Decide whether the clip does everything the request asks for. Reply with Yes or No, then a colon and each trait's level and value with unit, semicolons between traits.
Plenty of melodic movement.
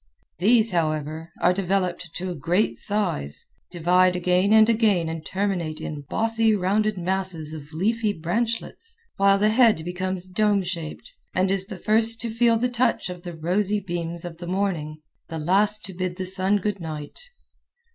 No: average, 3.6 semitones